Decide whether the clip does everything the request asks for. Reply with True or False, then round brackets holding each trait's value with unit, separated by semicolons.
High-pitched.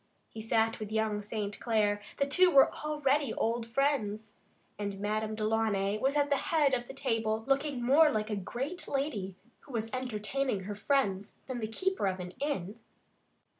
True (225 Hz)